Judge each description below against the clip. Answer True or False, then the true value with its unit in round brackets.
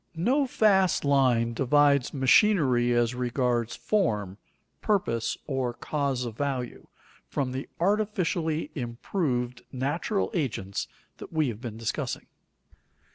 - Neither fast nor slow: False (110 wpm)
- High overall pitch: False (135 Hz)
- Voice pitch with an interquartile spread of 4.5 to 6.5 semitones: True (5.4 semitones)